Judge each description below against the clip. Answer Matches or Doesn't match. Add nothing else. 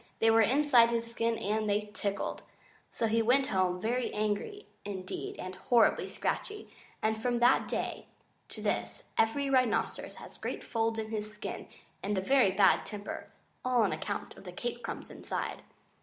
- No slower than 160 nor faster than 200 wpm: Matches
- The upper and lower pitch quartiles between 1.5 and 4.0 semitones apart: Matches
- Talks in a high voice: Matches